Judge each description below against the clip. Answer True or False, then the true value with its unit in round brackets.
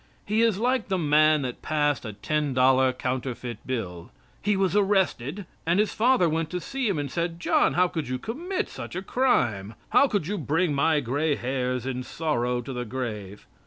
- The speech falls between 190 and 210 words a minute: True (195 wpm)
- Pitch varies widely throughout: True (6.9 semitones)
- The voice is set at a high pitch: False (150 Hz)